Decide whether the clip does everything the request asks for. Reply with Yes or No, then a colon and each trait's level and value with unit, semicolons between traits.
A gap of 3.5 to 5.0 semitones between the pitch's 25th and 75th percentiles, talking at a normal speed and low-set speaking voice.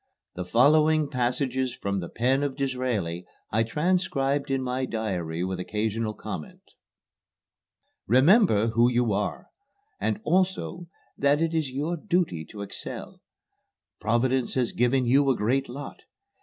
No: average, 4.6 semitones; slow, 130 wpm; low, 130 Hz